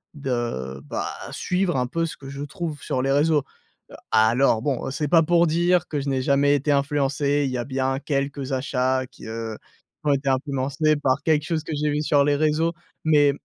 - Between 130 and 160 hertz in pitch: Yes, medium, 140 Hz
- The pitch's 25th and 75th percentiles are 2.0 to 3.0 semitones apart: Yes, narrow, 2.6 semitones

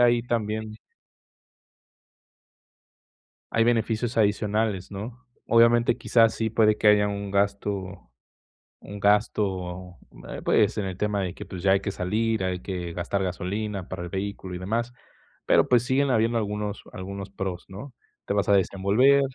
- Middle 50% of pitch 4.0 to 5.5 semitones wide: No, average, 2.9 semitones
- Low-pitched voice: Yes, low, 105 Hz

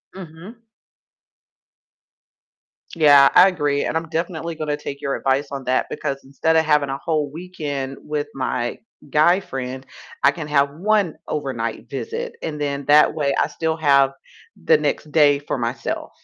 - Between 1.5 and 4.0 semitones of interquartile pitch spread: Yes, average, 2.8 semitones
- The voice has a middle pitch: Yes, medium, 150 Hz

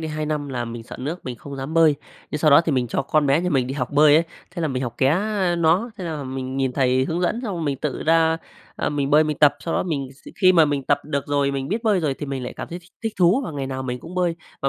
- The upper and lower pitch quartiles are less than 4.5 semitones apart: Yes, average, 3.8 semitones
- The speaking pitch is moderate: Yes, medium, 150 Hz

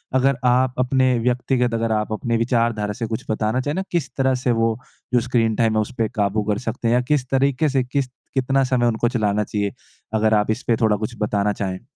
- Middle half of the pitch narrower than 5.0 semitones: Yes, average, 2.9 semitones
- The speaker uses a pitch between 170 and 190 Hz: No, low, 115 Hz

